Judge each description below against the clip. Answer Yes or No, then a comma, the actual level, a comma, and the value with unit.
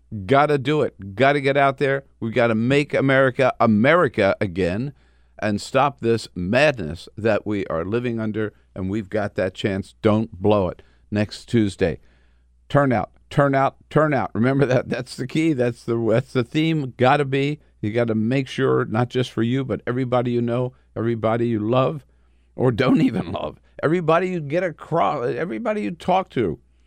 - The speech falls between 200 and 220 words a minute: No, average, 175 wpm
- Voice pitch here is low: Yes, low, 120 Hz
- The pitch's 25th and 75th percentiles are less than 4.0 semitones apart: No, average, 4.4 semitones